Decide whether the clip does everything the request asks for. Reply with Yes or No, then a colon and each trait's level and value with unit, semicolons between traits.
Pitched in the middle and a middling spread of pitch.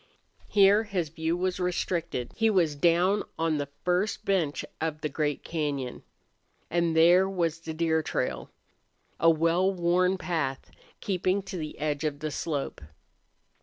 Yes: medium, 165 Hz; average, 3.0 semitones